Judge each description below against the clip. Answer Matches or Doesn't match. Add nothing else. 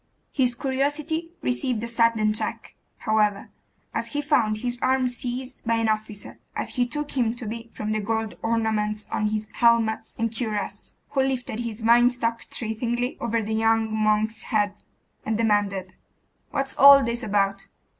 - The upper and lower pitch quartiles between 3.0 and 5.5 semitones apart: Doesn't match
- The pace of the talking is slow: Doesn't match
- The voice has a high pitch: Matches